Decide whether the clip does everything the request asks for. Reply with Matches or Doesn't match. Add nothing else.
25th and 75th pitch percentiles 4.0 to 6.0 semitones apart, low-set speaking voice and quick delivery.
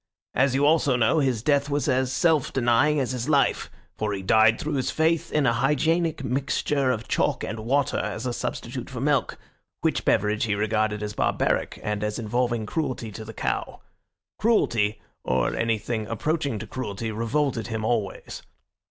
Doesn't match